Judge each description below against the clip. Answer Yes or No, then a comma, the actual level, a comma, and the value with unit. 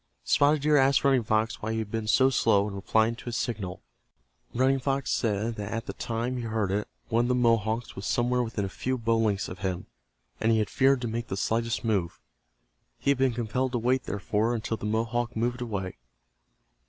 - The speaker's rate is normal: No, fast, 215 wpm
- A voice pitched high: No, low, 115 Hz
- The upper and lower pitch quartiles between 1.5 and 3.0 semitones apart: Yes, narrow, 2.4 semitones